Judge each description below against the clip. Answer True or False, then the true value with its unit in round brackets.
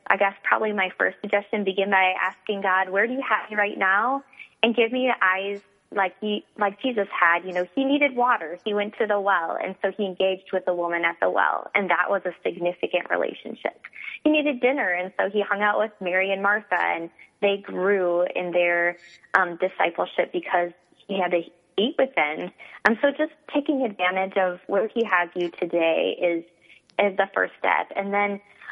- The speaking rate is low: False (205 wpm)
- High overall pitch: True (195 Hz)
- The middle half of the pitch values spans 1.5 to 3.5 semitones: True (3.0 semitones)